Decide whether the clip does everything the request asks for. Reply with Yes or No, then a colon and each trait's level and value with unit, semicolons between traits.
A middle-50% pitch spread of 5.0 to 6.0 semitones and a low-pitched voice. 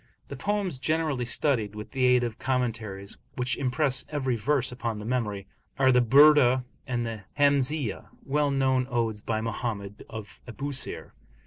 No: average, 3.5 semitones; low, 125 Hz